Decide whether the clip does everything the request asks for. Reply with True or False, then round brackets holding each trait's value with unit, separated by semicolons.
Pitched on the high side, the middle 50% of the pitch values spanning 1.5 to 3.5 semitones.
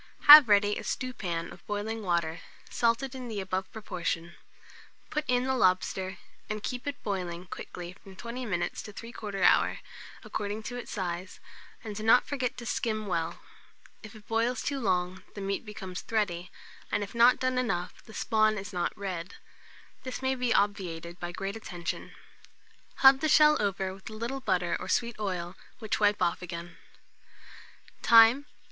False (205 Hz; 4.4 semitones)